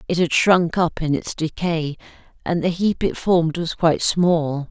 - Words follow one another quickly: No, average, 190 wpm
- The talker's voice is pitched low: No, medium, 165 Hz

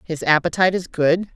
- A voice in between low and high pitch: Yes, medium, 170 Hz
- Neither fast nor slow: Yes, average, 180 wpm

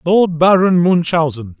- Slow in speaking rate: Yes, slow, 115 wpm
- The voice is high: No, medium, 170 Hz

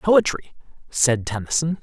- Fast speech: No, slow, 100 wpm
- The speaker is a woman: No, male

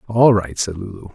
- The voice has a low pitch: Yes, low, 100 Hz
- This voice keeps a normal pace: No, fast, 210 wpm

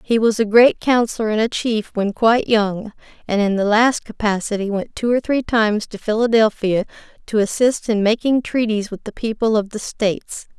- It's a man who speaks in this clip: No, female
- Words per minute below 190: No, average, 195 wpm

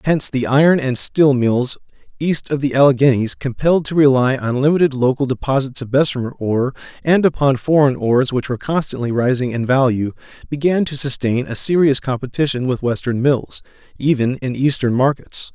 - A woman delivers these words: No, male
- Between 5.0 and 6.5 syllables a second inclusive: Yes, 5.4 syllables/s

